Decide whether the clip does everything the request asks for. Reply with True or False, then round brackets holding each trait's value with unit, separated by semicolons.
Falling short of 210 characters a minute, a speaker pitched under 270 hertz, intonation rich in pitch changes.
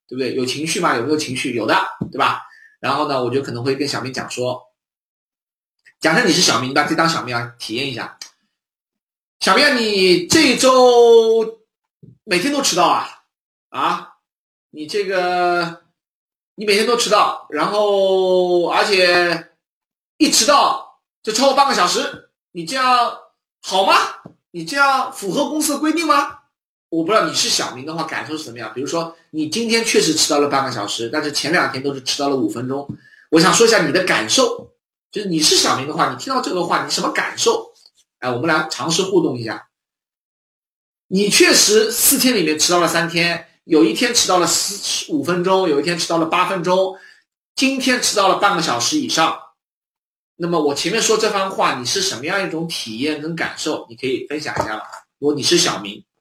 False (275 characters per minute; 185 Hz; 8.2 semitones)